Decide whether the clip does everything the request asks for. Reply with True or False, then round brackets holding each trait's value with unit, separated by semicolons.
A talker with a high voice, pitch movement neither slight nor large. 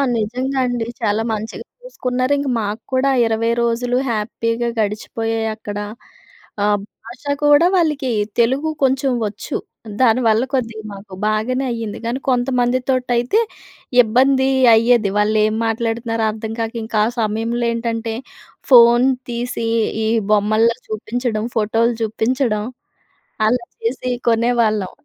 False (230 Hz; 2.3 semitones)